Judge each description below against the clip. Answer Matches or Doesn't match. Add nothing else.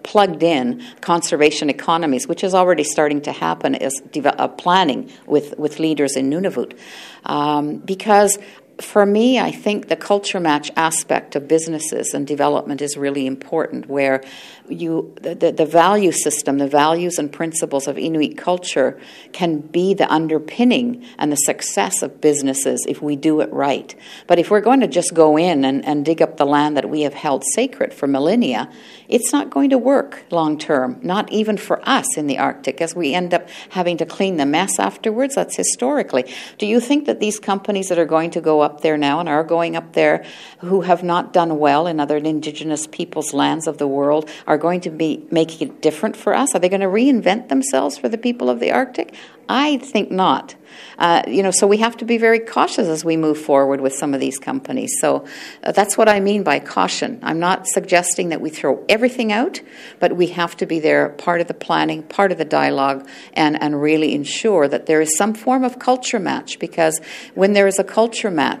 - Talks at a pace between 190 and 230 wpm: Matches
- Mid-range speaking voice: Matches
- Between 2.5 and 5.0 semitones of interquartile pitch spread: Doesn't match